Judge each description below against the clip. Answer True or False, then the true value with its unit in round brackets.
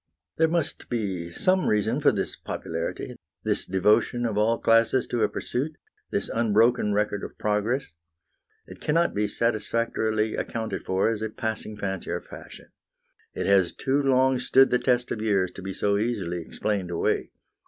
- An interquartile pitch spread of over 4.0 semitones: False (3.1 semitones)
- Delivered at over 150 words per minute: True (165 wpm)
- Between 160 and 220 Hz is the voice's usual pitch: False (110 Hz)